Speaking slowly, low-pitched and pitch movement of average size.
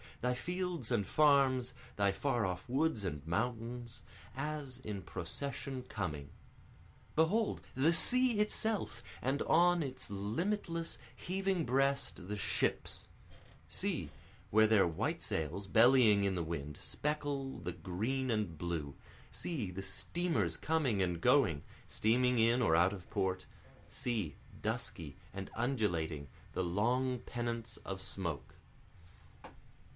No: slow, 120 wpm; low, 115 Hz; wide, 6.7 semitones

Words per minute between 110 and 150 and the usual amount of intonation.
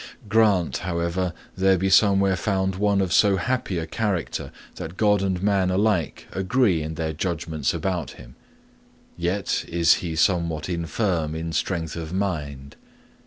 Yes: average, 145 wpm; average, 3.1 semitones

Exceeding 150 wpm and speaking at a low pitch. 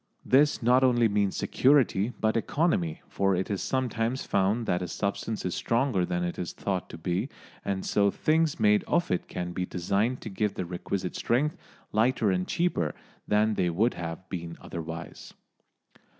Yes: average, 170 wpm; low, 100 Hz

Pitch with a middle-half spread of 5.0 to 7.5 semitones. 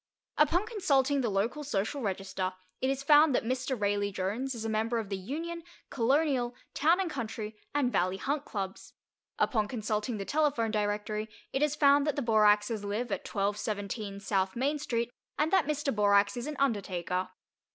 Yes: wide, 5.6 semitones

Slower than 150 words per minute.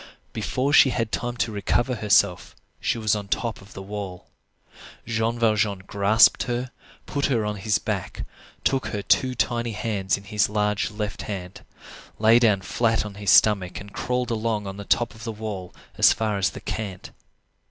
No: average, 180 wpm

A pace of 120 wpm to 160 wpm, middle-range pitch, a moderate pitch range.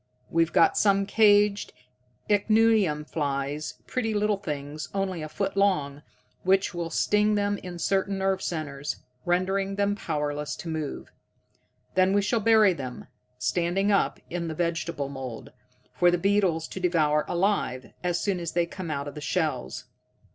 Yes: average, 155 wpm; medium, 175 Hz; average, 4.6 semitones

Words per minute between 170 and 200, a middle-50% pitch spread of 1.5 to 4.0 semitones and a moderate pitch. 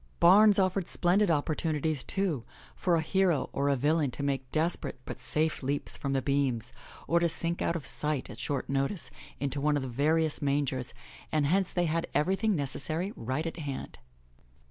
Yes: average, 185 wpm; average, 3.7 semitones; medium, 150 Hz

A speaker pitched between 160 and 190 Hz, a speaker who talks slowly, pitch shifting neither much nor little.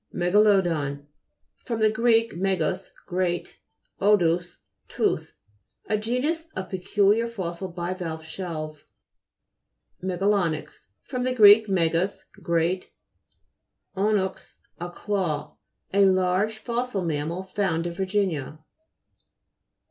Yes: medium, 185 Hz; slow, 90 wpm; average, 3.5 semitones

